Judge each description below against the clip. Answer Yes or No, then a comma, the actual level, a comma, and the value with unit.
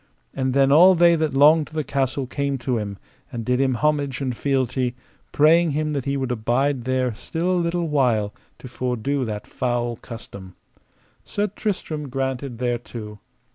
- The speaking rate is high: No, average, 170 wpm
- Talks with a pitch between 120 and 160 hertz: Yes, low, 135 Hz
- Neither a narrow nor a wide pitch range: Yes, average, 3.6 semitones